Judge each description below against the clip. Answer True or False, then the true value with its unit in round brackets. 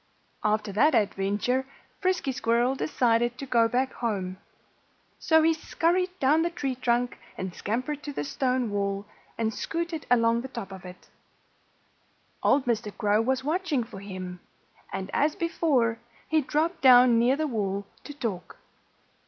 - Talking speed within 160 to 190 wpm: False (150 wpm)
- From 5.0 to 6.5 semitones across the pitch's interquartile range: True (5.6 semitones)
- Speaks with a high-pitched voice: True (245 Hz)